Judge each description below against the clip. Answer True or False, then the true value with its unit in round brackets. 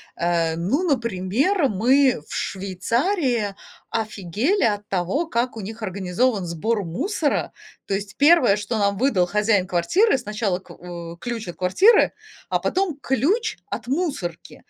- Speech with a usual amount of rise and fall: False (6.7 semitones)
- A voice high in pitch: True (215 Hz)